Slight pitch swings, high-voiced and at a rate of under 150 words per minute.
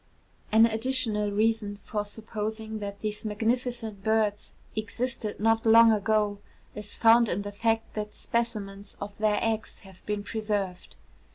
Yes: narrow, 1.6 semitones; high, 215 Hz; average, 140 wpm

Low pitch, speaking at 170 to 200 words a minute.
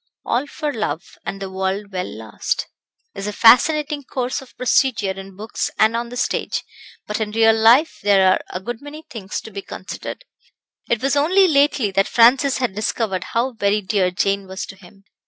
No: high, 220 Hz; average, 190 wpm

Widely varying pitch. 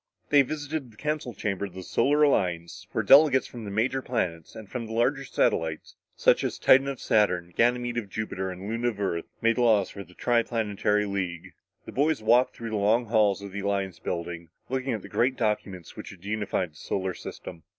No: average, 4.3 semitones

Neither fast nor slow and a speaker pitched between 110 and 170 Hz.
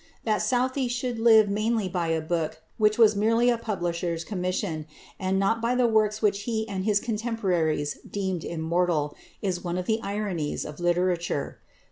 No: average, 165 wpm; high, 200 Hz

